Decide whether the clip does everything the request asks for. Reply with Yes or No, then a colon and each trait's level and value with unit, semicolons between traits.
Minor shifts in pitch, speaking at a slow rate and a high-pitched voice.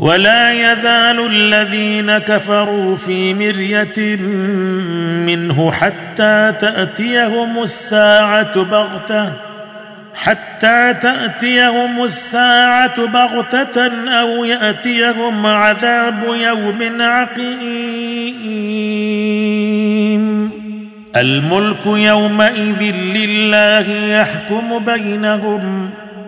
Yes: narrow, 2.0 semitones; slow, 55 wpm; high, 215 Hz